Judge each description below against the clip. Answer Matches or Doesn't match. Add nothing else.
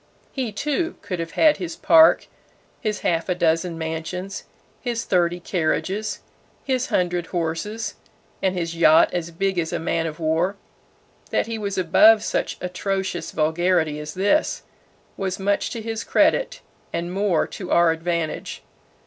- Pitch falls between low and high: Matches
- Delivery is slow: Doesn't match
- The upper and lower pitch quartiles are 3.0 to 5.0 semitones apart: Matches